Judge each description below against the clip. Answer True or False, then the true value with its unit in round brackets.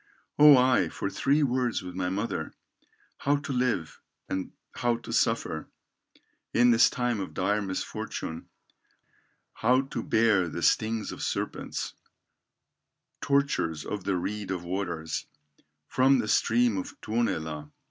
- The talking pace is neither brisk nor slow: False (125 wpm)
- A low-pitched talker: True (110 Hz)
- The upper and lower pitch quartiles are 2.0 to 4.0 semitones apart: False (5.1 semitones)